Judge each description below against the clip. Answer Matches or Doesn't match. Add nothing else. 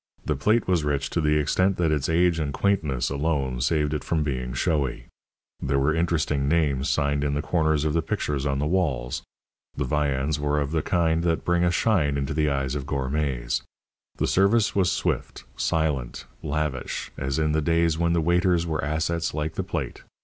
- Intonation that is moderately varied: Matches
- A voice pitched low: Matches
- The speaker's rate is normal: Matches